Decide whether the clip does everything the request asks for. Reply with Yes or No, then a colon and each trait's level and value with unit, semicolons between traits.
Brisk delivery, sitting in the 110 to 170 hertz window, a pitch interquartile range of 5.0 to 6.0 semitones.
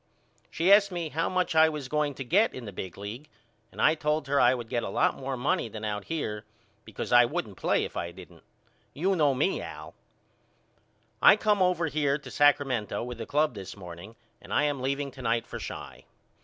Yes: fast, 210 wpm; medium, 140 Hz; wide, 5.4 semitones